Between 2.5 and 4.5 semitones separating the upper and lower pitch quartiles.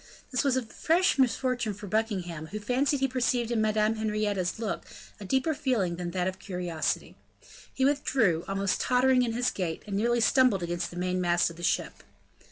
No: wide, 5.6 semitones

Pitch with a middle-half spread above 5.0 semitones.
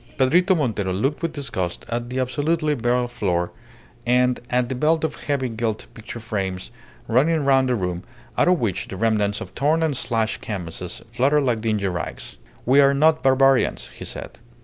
No: average, 4.6 semitones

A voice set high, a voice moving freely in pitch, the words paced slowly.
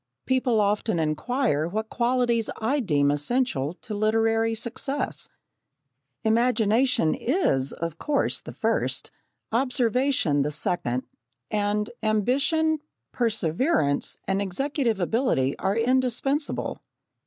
Yes: high, 225 Hz; wide, 6.0 semitones; slow, 95 wpm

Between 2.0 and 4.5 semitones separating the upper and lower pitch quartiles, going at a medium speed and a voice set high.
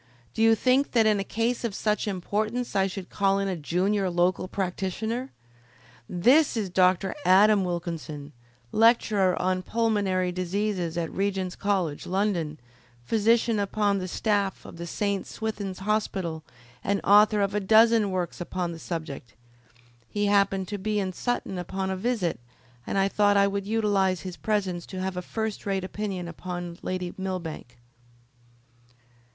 Yes: average, 2.7 semitones; average, 155 wpm; high, 195 Hz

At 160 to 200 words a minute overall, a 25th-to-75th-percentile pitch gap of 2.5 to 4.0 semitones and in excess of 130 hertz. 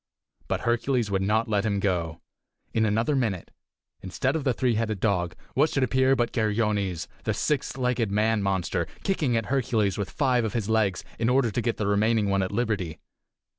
No: average, 190 wpm; average, 3.7 semitones; low, 110 Hz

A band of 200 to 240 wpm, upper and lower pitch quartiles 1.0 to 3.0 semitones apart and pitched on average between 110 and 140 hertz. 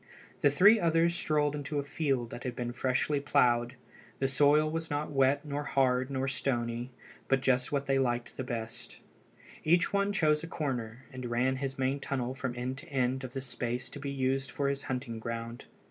No: average, 190 wpm; average, 2.7 semitones; low, 135 Hz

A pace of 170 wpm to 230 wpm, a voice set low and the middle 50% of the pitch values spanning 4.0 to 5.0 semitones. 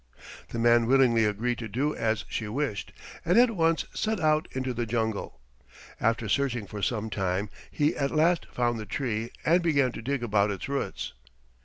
Yes: average, 180 wpm; low, 120 Hz; average, 4.6 semitones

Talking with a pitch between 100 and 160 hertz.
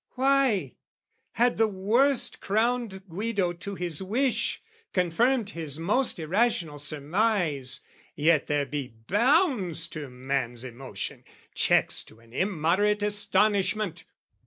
No: high, 190 Hz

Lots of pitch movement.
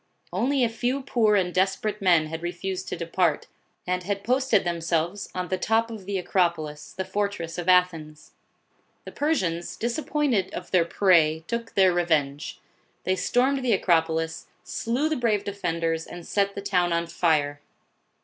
No: average, 4.1 semitones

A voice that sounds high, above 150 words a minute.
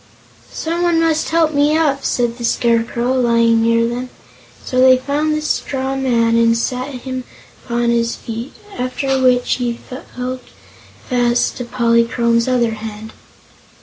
No: high, 245 Hz; average, 140 wpm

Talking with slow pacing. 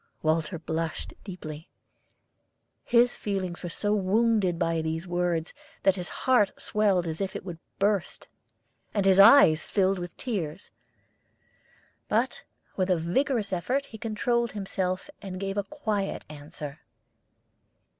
Yes: slow, 130 wpm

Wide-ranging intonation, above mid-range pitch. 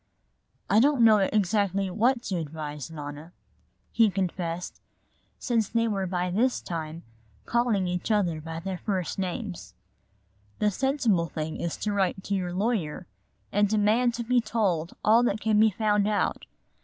No: average, 3.9 semitones; high, 200 Hz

